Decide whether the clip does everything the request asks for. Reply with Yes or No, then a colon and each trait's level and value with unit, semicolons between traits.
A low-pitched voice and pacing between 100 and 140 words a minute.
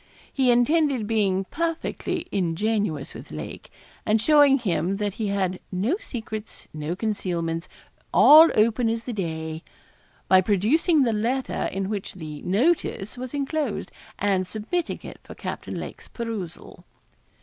No: high, 215 Hz; slow, 135 wpm